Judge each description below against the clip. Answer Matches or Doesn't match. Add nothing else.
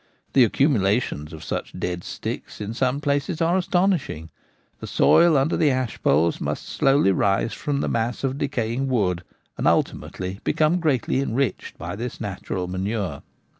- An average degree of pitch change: Doesn't match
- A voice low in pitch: Matches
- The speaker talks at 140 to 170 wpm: Matches